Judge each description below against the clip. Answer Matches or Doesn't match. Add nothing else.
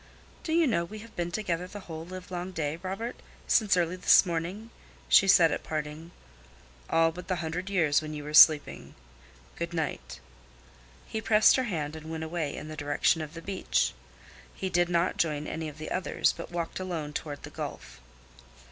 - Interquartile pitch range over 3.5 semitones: Doesn't match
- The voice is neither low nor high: Matches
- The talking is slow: Doesn't match